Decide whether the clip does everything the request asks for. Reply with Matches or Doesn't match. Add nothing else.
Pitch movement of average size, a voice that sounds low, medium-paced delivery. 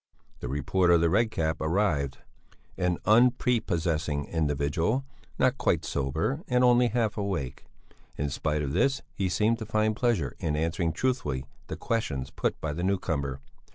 Doesn't match